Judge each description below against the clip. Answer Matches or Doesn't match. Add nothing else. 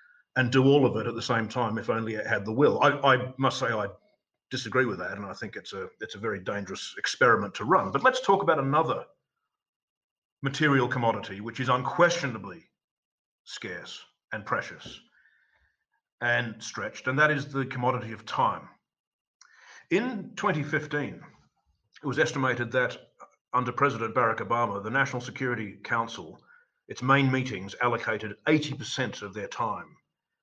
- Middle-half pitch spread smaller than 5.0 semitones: Matches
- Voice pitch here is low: Matches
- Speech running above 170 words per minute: Doesn't match